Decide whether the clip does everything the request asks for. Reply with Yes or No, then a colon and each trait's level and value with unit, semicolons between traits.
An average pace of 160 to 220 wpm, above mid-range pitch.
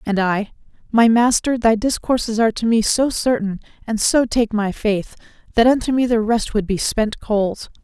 Yes: average, 190 wpm; high, 225 Hz